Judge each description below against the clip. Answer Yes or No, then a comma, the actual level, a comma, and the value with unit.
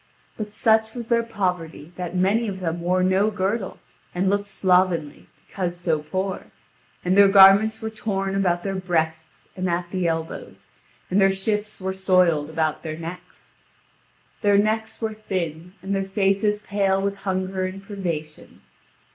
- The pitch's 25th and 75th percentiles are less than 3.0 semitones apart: Yes, narrow, 2.4 semitones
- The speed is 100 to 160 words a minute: Yes, average, 155 wpm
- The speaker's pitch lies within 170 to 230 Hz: Yes, high, 190 Hz